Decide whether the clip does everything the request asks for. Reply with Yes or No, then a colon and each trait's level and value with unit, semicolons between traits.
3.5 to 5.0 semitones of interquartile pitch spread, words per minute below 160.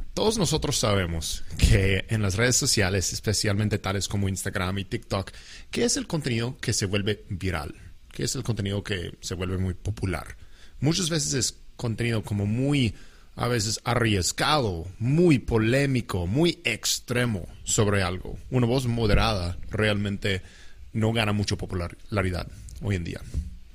Yes: average, 4.2 semitones; average, 145 wpm